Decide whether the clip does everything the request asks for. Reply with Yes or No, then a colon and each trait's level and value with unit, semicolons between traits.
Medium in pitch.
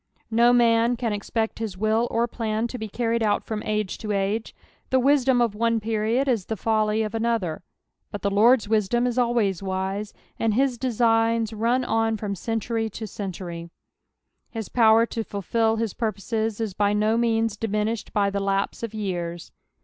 No: high, 220 Hz